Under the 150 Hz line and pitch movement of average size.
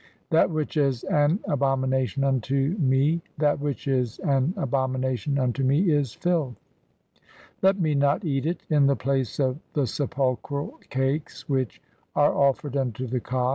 No: medium, 140 Hz; narrow, 2.1 semitones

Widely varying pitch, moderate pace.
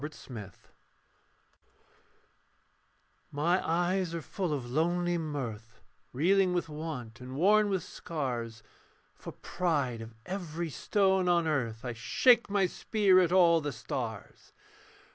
No: wide, 6.4 semitones; slow, 125 wpm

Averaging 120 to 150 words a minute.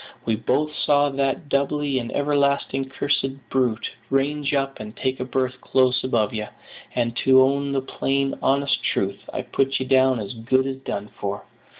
No: average, 175 wpm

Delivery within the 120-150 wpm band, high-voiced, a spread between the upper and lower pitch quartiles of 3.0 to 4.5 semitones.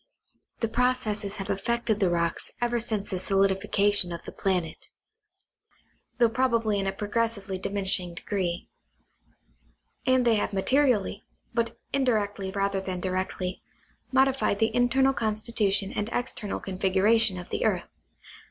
Yes: slow, 135 wpm; high, 205 Hz; average, 3.4 semitones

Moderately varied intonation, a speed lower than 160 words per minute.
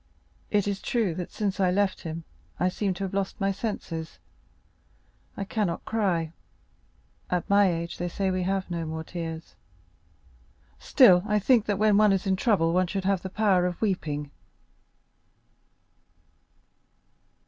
Yes: average, 3.3 semitones; average, 150 wpm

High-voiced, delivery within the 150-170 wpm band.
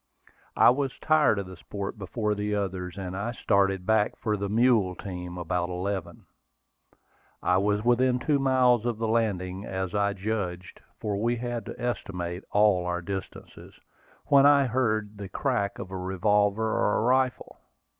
No: low, 105 Hz; average, 165 wpm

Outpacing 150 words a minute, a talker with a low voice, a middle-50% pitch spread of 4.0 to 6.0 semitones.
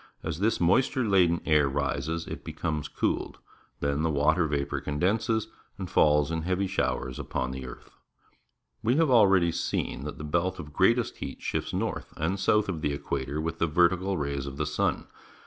Yes: average, 180 wpm; very low, 80 Hz; average, 4.7 semitones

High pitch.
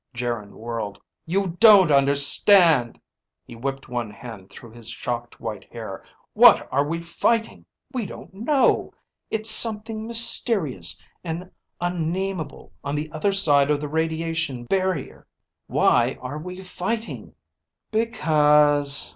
No: medium, 155 Hz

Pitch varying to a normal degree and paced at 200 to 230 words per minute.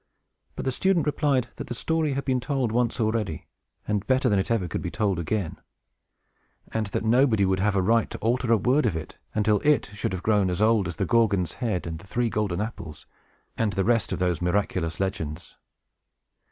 Yes: average, 4.5 semitones; fast, 205 wpm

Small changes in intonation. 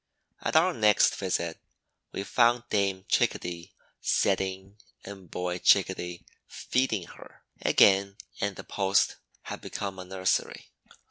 Yes: narrow, 1.6 semitones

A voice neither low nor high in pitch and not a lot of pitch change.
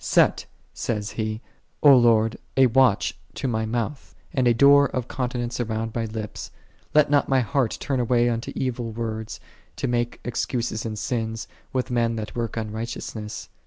No: low, 120 Hz; narrow, 2.3 semitones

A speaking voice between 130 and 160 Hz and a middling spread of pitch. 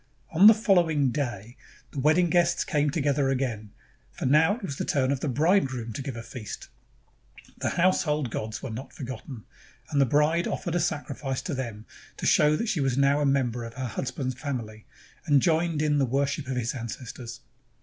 Yes: medium, 140 Hz; average, 3.7 semitones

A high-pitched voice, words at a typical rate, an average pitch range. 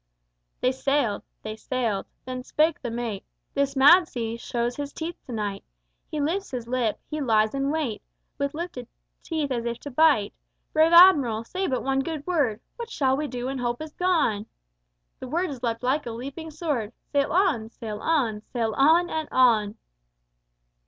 Yes: very high, 265 Hz; average, 175 wpm; average, 5.0 semitones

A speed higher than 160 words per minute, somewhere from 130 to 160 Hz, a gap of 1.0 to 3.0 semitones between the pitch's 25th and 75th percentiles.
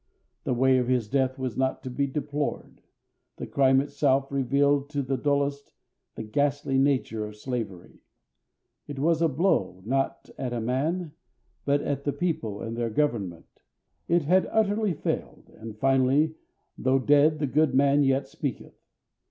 No: average, 155 wpm; low, 135 Hz; narrow, 2.4 semitones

